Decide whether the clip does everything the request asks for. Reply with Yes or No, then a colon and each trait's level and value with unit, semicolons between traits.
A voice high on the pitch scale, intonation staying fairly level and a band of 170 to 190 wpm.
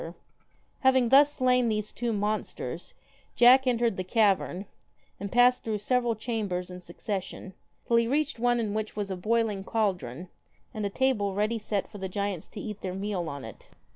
No: high, 210 Hz; average, 3.7 semitones; average, 180 wpm